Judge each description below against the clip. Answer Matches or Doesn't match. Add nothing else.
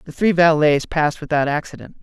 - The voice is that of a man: Matches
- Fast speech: Doesn't match